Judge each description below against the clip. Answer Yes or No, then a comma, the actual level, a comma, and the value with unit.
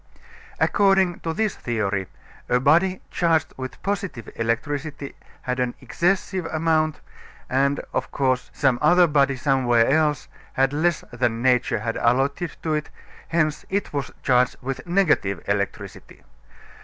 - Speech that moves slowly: Yes, slow, 130 wpm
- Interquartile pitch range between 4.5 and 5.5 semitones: Yes, average, 4.8 semitones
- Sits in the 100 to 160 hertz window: Yes, medium, 140 Hz